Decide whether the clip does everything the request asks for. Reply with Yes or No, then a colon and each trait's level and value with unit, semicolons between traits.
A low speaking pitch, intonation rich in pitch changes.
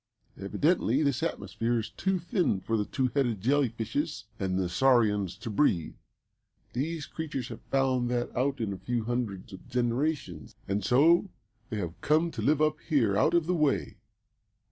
Yes: low, 125 Hz; wide, 6.0 semitones